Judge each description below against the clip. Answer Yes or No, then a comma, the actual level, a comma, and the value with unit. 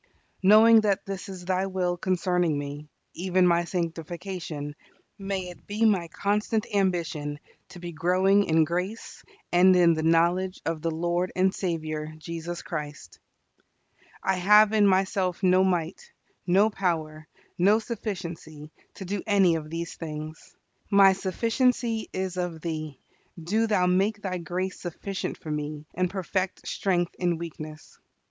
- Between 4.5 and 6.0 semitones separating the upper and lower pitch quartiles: No, average, 2.9 semitones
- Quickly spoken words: No, average, 140 wpm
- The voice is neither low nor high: Yes, medium, 180 Hz